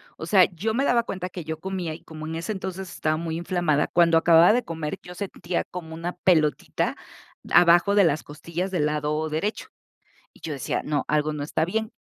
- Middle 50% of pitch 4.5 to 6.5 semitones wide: No, average, 3.0 semitones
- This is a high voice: No, medium, 170 Hz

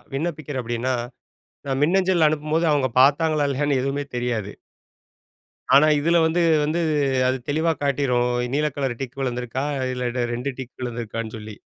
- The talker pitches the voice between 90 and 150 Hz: Yes, low, 135 Hz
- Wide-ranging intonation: No, average, 3.7 semitones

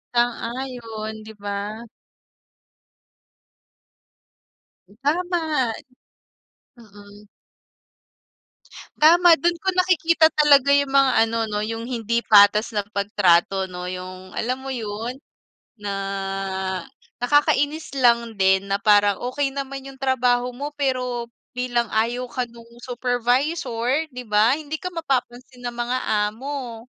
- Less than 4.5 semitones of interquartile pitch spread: Yes, average, 4.1 semitones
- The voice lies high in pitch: Yes, high, 245 Hz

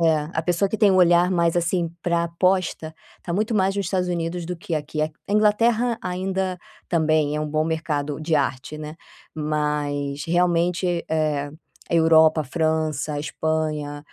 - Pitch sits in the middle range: Yes, medium, 165 Hz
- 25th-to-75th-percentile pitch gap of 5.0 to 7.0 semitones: No, average, 2.8 semitones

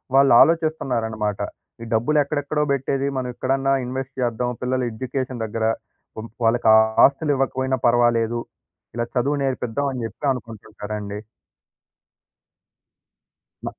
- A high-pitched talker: No, low, 125 Hz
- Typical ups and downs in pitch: Yes, average, 3.1 semitones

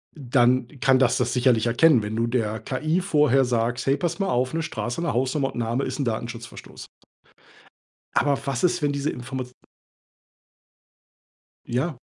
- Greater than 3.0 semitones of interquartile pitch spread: Yes, average, 3.4 semitones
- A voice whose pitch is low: Yes, low, 130 Hz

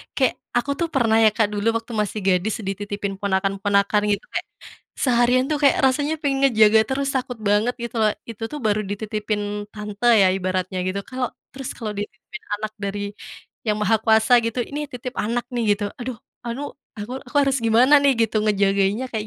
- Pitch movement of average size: Yes, average, 3.5 semitones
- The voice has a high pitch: Yes, high, 220 Hz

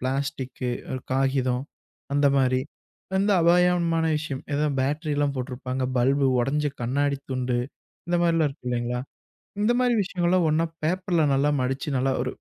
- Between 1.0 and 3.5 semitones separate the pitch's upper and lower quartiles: No, average, 4.3 semitones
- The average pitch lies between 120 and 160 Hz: Yes, medium, 140 Hz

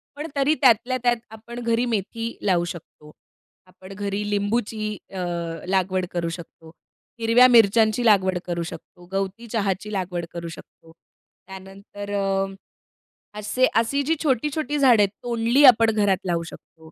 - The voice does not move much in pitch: No, average, 3.9 semitones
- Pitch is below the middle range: No, high, 205 Hz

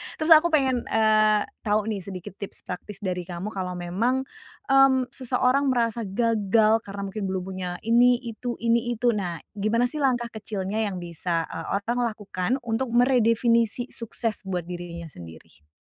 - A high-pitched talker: Yes, high, 215 Hz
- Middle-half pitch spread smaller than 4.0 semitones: No, average, 4.3 semitones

